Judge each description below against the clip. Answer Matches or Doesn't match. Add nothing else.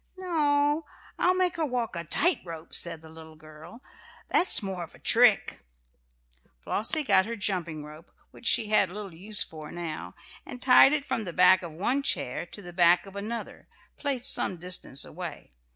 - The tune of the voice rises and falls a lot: Matches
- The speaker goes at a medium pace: Matches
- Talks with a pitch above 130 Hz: Matches